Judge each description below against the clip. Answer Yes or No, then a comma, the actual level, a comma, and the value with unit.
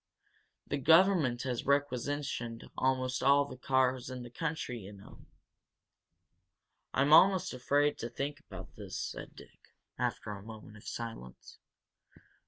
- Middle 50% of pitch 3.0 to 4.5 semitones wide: Yes, average, 3.5 semitones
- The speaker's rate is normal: No, slow, 130 wpm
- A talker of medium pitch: No, low, 130 Hz